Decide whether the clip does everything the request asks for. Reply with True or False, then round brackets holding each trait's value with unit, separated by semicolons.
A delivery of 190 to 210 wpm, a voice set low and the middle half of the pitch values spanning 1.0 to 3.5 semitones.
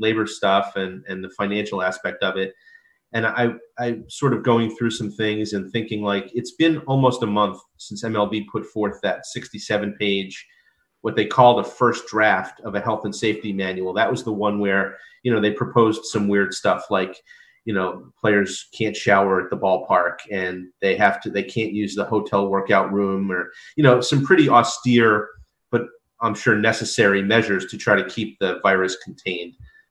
True (195 wpm; 105 Hz; 2.9 semitones)